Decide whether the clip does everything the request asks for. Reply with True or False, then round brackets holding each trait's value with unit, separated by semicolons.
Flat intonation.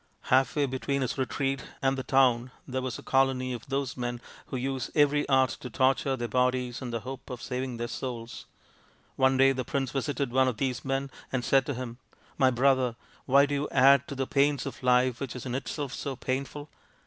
True (1.3 semitones)